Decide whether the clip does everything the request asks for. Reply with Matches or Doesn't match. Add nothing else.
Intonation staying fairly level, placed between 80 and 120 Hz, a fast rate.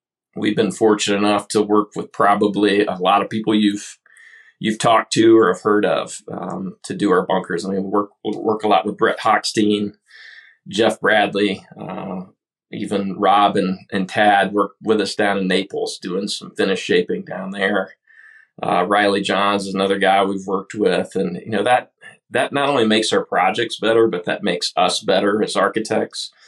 Doesn't match